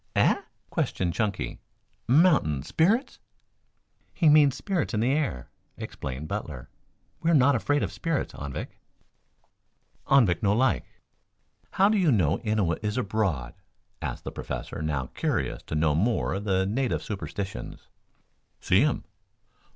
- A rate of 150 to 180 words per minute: No, slow, 135 wpm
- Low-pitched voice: Yes, low, 105 Hz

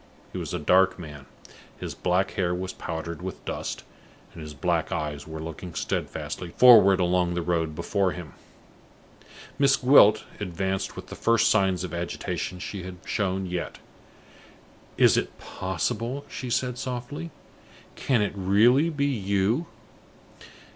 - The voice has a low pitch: Yes, very low, 95 Hz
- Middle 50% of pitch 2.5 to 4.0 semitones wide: No, average, 4.9 semitones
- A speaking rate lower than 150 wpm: Yes, average, 140 wpm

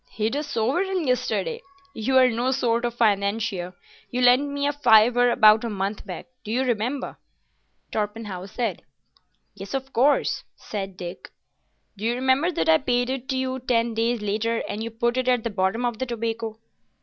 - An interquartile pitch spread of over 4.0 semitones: No, average, 3.2 semitones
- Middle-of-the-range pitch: No, high, 235 Hz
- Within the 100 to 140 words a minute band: No, average, 165 wpm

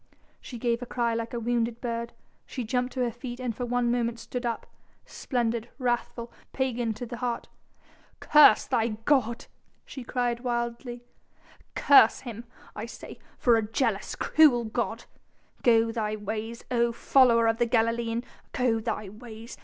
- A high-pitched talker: Yes, high, 235 Hz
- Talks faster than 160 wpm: No, average, 155 wpm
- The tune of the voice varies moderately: No, narrow, 1.4 semitones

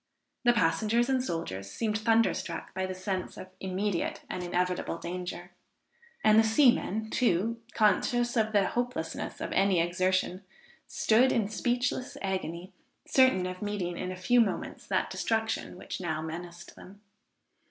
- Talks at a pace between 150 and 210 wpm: No, average, 140 wpm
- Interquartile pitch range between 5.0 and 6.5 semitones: No, average, 4.0 semitones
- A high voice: Yes, high, 195 Hz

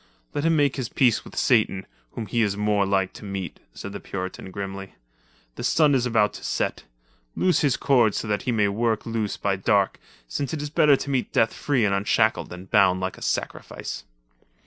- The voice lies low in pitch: Yes, low, 105 Hz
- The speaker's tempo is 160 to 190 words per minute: No, fast, 205 wpm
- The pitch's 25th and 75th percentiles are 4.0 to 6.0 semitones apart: Yes, average, 4.8 semitones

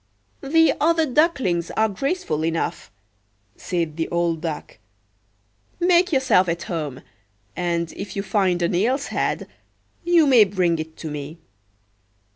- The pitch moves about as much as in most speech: No, wide, 8.7 semitones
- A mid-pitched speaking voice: Yes, medium, 180 Hz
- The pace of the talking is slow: Yes, slow, 130 wpm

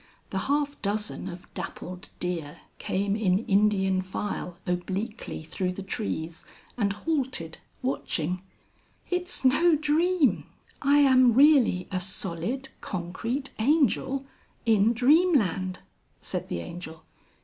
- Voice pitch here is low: No, high, 210 Hz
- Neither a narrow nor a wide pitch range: No, wide, 7.0 semitones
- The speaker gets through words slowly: Yes, slow, 115 wpm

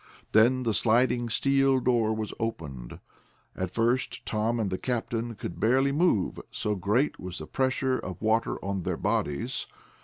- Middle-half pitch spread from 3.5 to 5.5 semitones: Yes, average, 4.0 semitones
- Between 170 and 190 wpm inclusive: No, average, 155 wpm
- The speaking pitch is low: Yes, low, 115 Hz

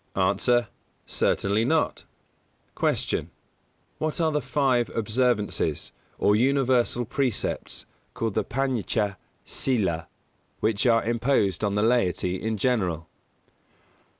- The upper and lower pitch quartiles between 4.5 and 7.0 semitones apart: No, average, 4.0 semitones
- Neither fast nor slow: No, slow, 110 wpm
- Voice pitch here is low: Yes, low, 115 Hz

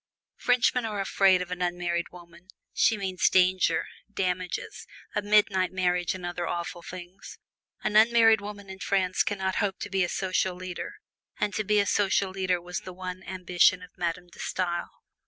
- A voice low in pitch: No, medium, 185 Hz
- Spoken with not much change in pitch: Yes, narrow, 2.0 semitones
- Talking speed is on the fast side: No, average, 175 wpm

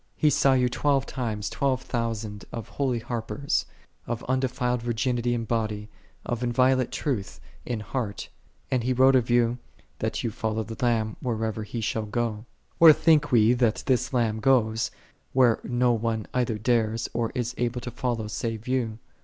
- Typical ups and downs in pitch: No, narrow, 2.2 semitones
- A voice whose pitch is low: Yes, low, 120 Hz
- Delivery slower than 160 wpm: No, average, 165 wpm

